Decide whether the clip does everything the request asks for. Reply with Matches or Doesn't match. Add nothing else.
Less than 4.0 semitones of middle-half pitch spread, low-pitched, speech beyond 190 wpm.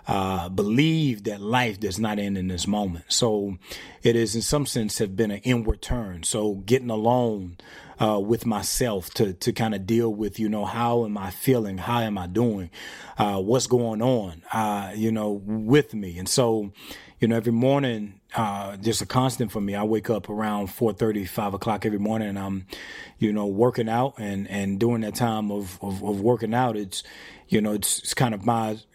Matches